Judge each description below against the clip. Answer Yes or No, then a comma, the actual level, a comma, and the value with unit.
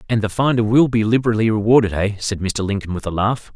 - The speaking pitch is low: Yes, low, 110 Hz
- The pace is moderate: No, fast, 235 wpm